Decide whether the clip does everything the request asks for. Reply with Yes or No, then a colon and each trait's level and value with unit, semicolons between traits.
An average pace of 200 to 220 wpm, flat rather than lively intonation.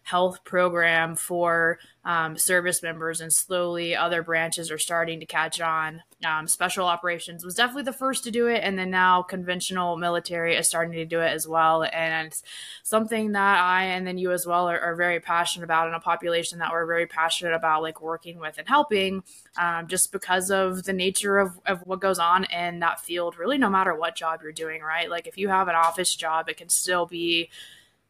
Yes: fast, 205 wpm; narrow, 1.9 semitones